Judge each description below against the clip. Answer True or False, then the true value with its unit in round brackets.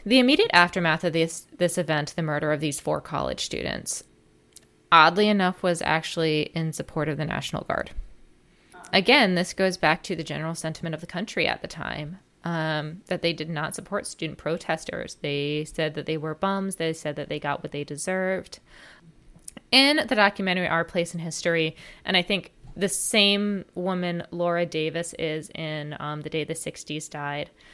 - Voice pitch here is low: False (165 Hz)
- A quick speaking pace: False (180 wpm)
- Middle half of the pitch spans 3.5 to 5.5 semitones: False (3.0 semitones)